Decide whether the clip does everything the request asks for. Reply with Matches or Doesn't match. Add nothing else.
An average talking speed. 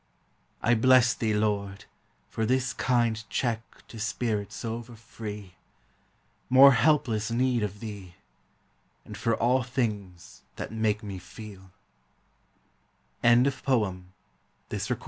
Doesn't match